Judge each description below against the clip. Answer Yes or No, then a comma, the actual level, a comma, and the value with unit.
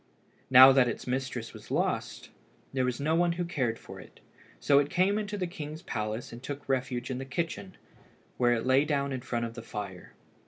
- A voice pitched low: Yes, low, 130 Hz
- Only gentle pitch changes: No, average, 4.1 semitones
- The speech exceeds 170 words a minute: Yes, fast, 205 wpm